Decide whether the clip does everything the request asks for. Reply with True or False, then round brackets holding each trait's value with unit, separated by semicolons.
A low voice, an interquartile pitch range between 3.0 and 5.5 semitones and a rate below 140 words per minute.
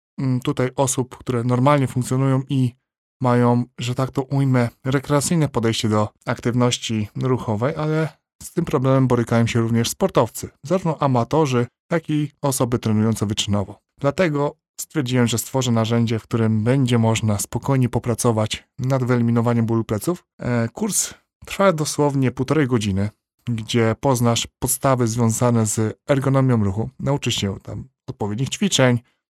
True (125 Hz; 3.3 semitones; 130 wpm)